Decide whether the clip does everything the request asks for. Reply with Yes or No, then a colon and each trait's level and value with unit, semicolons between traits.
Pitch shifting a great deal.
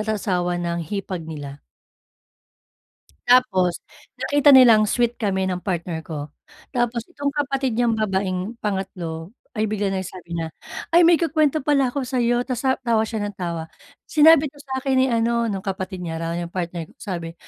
Yes: wide, 6.1 semitones